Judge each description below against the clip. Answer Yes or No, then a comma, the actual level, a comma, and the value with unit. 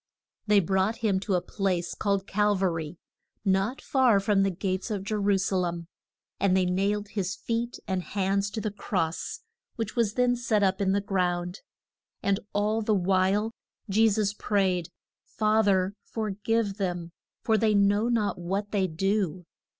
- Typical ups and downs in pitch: No, narrow, 2.2 semitones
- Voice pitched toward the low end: No, high, 200 Hz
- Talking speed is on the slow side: No, average, 175 wpm